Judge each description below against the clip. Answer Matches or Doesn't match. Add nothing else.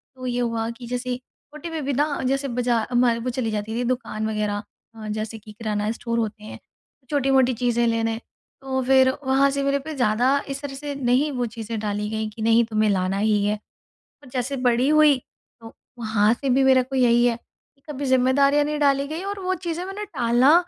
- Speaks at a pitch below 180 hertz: Doesn't match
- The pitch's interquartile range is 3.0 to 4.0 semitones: Matches